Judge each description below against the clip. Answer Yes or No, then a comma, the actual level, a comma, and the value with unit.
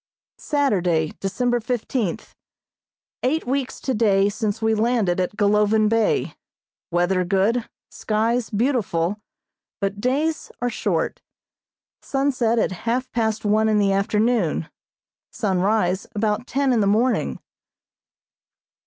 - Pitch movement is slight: No, average, 3.6 semitones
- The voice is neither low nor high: No, high, 220 Hz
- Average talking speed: No, slow, 110 wpm